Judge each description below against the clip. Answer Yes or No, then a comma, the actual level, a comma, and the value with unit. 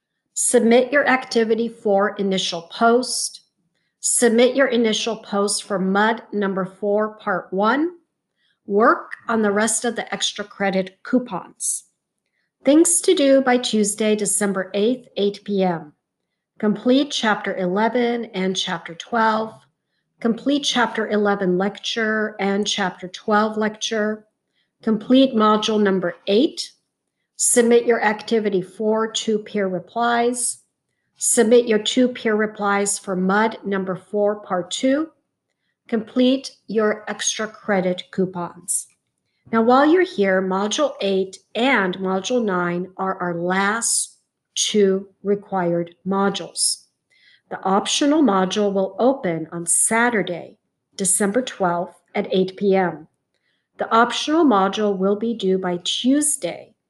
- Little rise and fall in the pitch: No, average, 3.7 semitones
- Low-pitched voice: No, high, 210 Hz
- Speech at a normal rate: No, slow, 115 wpm